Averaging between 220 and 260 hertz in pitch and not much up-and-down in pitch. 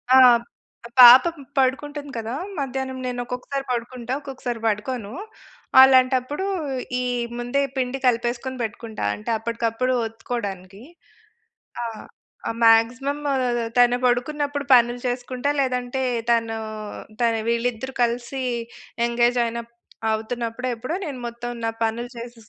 Yes: high, 245 Hz; narrow, 2.1 semitones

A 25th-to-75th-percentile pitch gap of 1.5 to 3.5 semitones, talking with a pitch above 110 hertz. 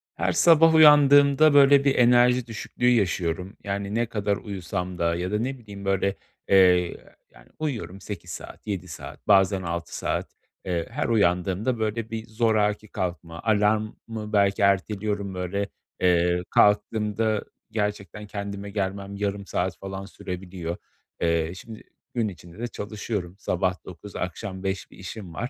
No: average, 3.2 semitones; low, 100 Hz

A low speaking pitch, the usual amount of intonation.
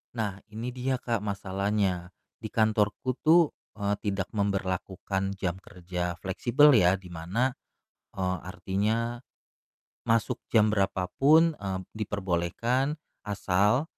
Yes: low, 100 Hz; average, 3.7 semitones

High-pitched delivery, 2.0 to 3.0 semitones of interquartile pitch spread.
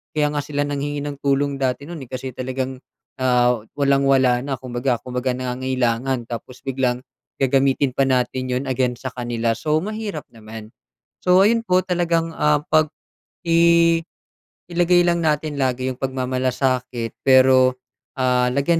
No: low, 130 Hz; narrow, 2.6 semitones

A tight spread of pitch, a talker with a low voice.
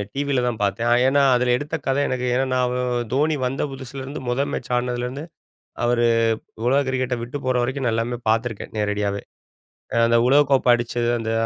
Yes: narrow, 2.1 semitones; low, 125 Hz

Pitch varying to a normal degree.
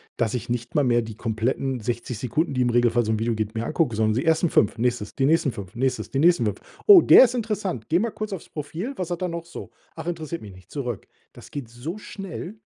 No: wide, 6.7 semitones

